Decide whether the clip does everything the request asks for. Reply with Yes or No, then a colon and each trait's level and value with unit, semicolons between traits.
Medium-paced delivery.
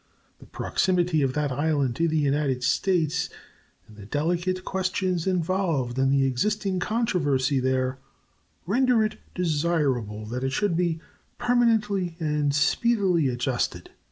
No: slow, 130 wpm